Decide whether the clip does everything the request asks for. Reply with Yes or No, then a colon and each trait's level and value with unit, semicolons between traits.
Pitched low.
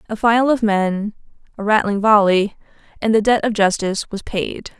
No: high, 210 Hz